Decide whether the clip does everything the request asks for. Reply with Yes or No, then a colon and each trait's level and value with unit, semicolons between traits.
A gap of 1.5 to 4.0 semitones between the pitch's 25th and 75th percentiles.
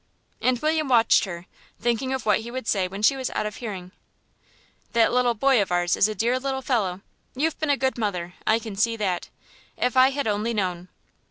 No: average, 4.8 semitones